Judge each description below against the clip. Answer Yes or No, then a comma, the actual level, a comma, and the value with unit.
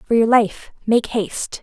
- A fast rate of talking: No, average, 185 wpm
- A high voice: Yes, high, 220 Hz